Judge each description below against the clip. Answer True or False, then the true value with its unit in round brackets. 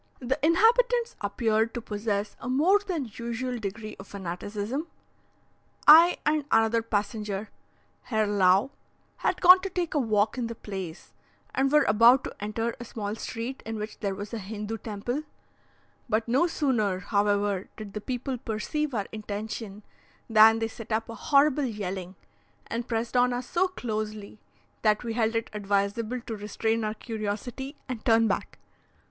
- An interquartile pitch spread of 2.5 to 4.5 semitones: True (3.5 semitones)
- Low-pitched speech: False (225 Hz)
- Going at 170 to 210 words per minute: False (160 wpm)